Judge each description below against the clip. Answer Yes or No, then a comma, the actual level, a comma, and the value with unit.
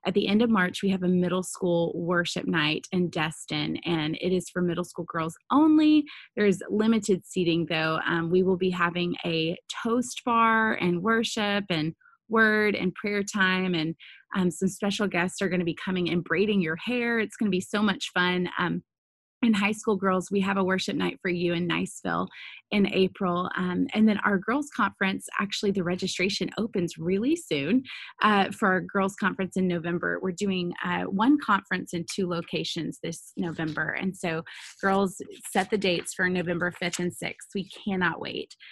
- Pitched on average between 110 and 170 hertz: No, medium, 185 Hz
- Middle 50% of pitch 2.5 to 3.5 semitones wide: Yes, average, 2.9 semitones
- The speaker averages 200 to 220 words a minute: No, average, 190 wpm